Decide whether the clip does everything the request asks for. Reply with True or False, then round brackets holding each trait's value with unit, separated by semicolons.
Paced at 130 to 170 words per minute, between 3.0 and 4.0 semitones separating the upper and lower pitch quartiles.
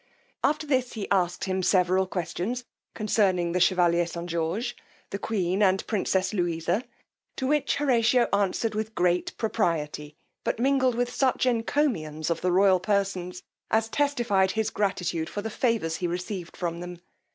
False (150 wpm; 4.5 semitones)